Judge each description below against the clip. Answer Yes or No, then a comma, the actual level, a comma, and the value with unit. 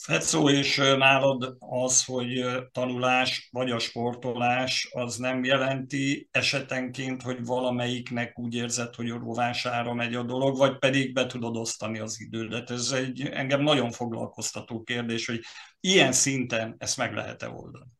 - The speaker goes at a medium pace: Yes, average, 145 wpm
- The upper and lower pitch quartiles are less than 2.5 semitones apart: Yes, narrow, 1.6 semitones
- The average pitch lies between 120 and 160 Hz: Yes, low, 125 Hz